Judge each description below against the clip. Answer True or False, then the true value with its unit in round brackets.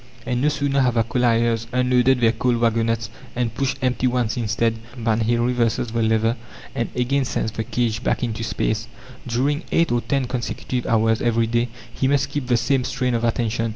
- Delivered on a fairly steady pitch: True (1.8 semitones)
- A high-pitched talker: False (120 Hz)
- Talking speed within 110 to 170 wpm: False (190 wpm)